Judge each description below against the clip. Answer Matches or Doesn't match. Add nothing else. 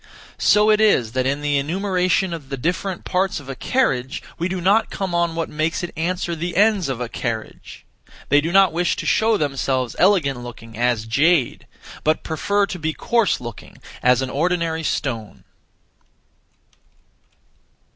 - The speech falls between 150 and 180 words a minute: Matches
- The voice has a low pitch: Doesn't match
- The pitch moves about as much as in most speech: Doesn't match